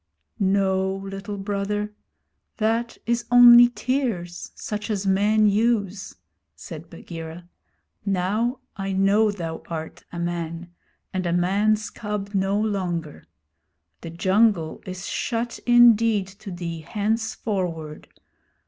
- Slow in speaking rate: Yes, slow, 110 wpm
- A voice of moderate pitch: No, high, 200 Hz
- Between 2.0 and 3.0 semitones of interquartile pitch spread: No, average, 3.4 semitones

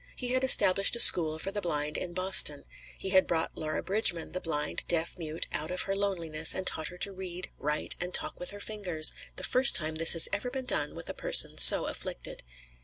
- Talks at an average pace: No, fast, 220 wpm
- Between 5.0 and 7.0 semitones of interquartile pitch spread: No, average, 3.8 semitones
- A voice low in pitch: No, medium, 180 Hz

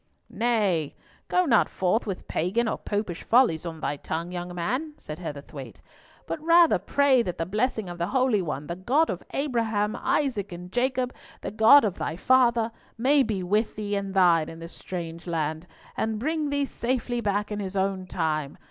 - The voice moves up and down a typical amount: No, wide, 6.1 semitones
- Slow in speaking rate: No, average, 185 wpm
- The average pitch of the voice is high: Yes, high, 205 Hz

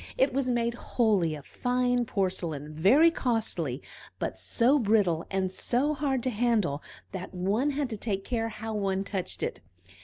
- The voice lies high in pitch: Yes, high, 220 Hz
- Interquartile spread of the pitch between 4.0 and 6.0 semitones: Yes, average, 4.8 semitones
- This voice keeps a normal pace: Yes, average, 160 wpm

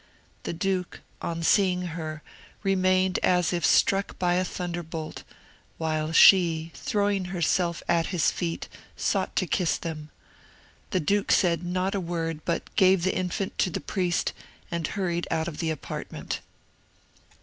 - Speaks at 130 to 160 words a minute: Yes, average, 145 wpm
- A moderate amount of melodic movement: No, narrow, 2.1 semitones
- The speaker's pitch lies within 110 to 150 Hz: No, medium, 175 Hz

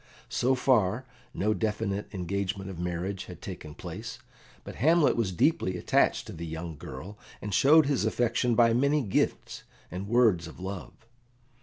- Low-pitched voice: Yes, low, 100 Hz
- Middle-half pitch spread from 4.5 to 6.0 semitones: Yes, average, 5.1 semitones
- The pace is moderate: Yes, average, 155 wpm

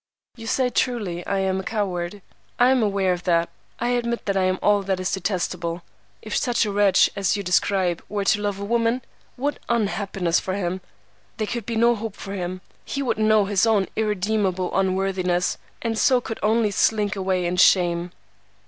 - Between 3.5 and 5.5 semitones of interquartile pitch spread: No, average, 3.1 semitones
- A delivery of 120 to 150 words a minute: No, average, 190 wpm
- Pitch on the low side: No, high, 200 Hz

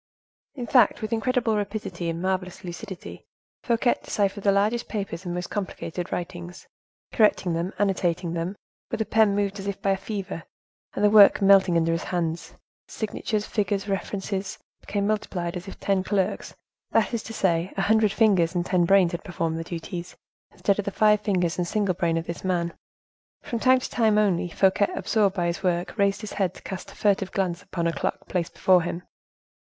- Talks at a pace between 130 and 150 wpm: No, average, 190 wpm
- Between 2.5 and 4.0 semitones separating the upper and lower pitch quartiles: Yes, average, 3.0 semitones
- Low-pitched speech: No, high, 195 Hz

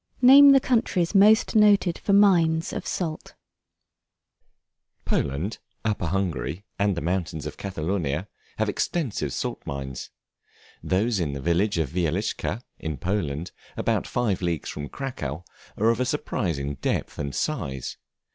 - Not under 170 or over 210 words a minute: No, slow, 135 wpm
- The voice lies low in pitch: Yes, very low, 95 Hz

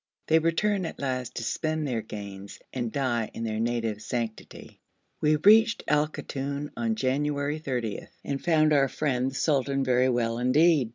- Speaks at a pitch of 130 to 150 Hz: Yes, low, 135 Hz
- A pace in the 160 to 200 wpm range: Yes, average, 165 wpm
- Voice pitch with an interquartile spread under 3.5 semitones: No, average, 4.2 semitones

